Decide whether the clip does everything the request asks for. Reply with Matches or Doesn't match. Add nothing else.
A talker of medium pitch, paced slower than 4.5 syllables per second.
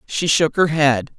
Matches